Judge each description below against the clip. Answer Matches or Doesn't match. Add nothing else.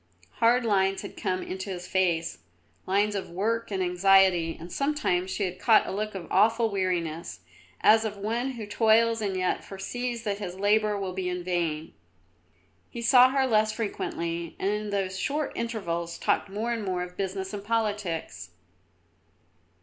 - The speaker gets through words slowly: Doesn't match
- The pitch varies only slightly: Doesn't match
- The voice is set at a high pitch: Matches